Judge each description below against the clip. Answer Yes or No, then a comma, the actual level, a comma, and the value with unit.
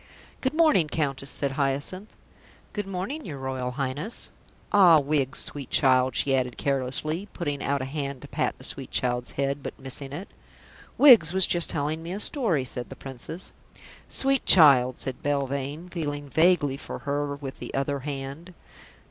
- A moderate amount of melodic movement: Yes, average, 4.2 semitones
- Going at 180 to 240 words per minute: No, average, 165 wpm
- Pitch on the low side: No, medium, 145 Hz